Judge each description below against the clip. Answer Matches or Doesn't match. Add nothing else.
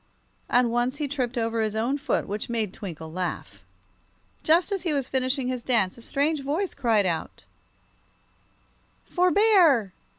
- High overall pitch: Matches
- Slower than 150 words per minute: Doesn't match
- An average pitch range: Matches